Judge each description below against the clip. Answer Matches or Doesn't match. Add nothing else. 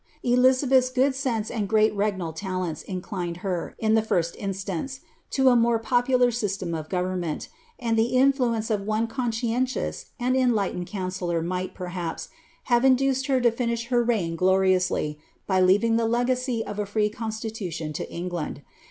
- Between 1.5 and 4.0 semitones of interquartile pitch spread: Doesn't match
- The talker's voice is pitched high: Matches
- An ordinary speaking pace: Matches